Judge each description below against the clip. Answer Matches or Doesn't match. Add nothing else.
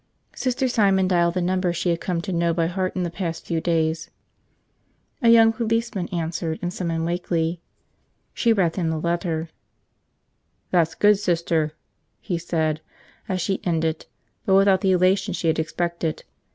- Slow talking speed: Doesn't match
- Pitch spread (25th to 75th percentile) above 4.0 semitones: Doesn't match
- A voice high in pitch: Doesn't match